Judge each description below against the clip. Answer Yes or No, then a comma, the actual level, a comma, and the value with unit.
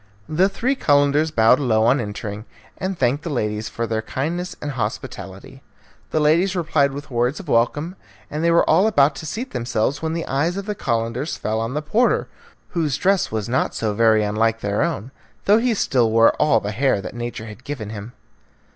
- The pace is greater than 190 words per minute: Yes, average, 200 wpm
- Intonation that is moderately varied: No, wide, 6.2 semitones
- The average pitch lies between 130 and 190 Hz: Yes, low, 135 Hz